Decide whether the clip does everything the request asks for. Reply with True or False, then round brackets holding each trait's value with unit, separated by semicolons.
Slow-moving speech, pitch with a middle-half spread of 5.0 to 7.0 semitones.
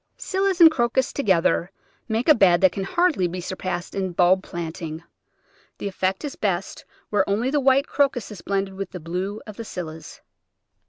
False (175 wpm; 5.4 semitones)